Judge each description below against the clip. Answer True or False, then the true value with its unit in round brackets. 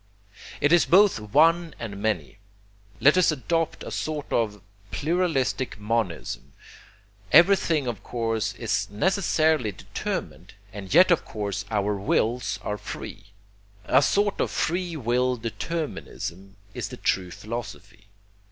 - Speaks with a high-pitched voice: False (120 Hz)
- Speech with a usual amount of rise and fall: False (7.8 semitones)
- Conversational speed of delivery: False (125 wpm)